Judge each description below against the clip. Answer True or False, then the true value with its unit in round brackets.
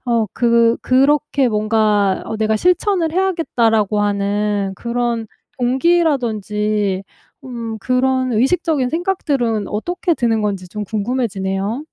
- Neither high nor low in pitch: False (230 Hz)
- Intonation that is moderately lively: True (4.1 semitones)